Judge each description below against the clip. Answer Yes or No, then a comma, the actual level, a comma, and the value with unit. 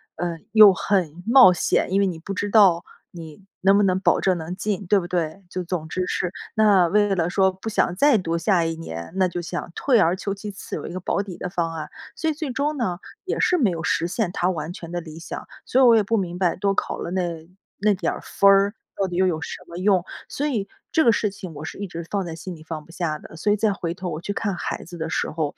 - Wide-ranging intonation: No, average, 3.2 semitones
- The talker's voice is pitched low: No, medium, 185 Hz